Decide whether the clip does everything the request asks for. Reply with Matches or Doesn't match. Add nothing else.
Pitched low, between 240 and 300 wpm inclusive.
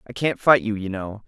Matches